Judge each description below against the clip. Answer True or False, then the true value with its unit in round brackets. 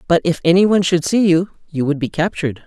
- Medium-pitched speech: True (170 Hz)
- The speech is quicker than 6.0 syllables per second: True (6.2 syllables/s)